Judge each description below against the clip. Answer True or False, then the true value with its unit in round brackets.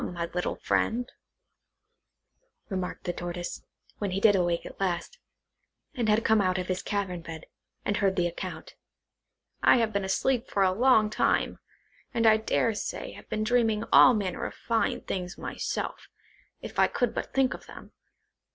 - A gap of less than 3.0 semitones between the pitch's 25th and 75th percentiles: False (3.7 semitones)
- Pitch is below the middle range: False (200 Hz)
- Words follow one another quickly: False (175 wpm)